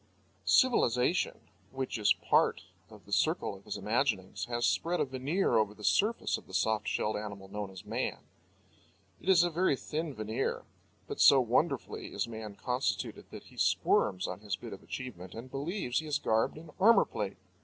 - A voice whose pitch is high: No, low, 120 Hz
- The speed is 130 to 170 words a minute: No, average, 180 wpm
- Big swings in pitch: Yes, wide, 6.4 semitones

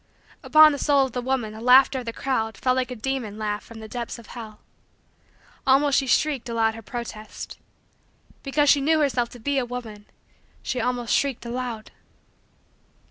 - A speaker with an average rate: Yes, average, 180 wpm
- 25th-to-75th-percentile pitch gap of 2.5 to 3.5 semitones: Yes, average, 3.2 semitones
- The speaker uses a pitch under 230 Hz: No, high, 245 Hz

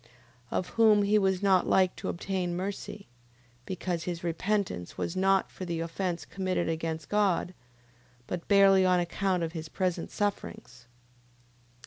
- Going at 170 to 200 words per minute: No, average, 140 wpm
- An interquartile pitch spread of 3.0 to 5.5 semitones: No, narrow, 2.4 semitones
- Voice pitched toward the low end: No, medium, 185 Hz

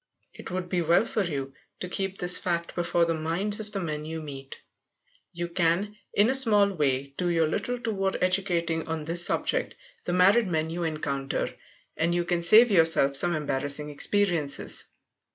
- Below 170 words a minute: No, average, 175 wpm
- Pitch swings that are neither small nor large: Yes, average, 3.6 semitones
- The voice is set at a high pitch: No, medium, 170 Hz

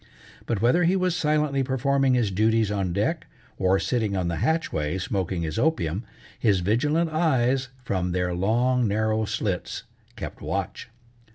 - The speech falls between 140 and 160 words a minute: Yes, average, 150 wpm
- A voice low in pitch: Yes, low, 115 Hz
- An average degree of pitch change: No, wide, 6.2 semitones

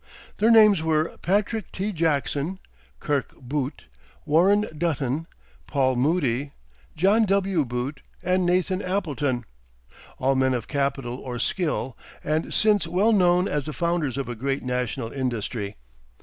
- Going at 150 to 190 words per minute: No, slow, 135 wpm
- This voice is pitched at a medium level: Yes, medium, 150 Hz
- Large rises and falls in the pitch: Yes, wide, 5.8 semitones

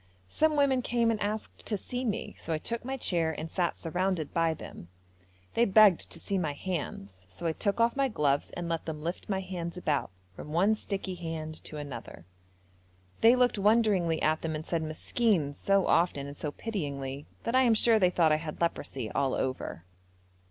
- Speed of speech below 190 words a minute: No, average, 195 wpm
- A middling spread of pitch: No, wide, 5.8 semitones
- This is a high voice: No, medium, 170 Hz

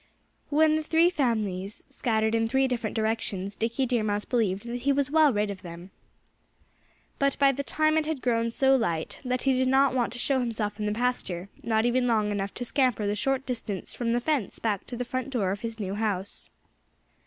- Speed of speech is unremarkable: No, fast, 210 wpm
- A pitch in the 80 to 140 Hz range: No, high, 235 Hz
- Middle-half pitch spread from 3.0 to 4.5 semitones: Yes, average, 4.2 semitones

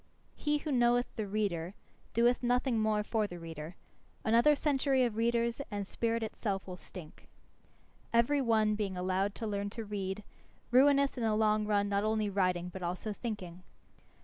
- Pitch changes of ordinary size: Yes, average, 3.5 semitones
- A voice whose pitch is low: No, high, 215 Hz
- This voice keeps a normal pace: Yes, average, 165 wpm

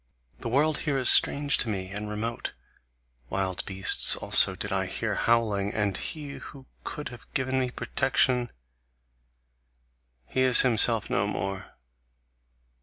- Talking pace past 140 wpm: No, slow, 135 wpm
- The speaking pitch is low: Yes, low, 115 Hz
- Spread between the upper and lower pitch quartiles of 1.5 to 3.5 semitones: No, average, 4.5 semitones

